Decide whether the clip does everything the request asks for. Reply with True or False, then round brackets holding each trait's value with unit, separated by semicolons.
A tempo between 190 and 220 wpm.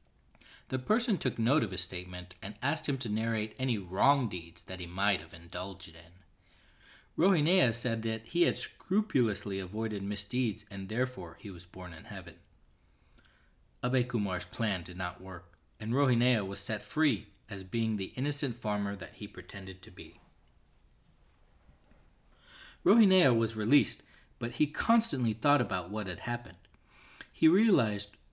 False (150 wpm)